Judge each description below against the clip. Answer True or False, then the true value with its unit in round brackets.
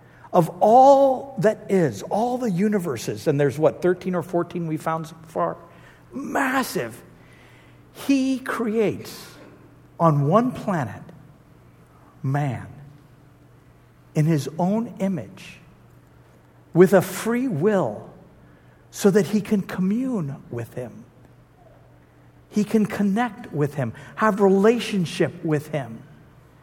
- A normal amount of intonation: False (7.5 semitones)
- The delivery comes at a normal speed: False (110 wpm)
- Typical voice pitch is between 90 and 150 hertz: False (175 Hz)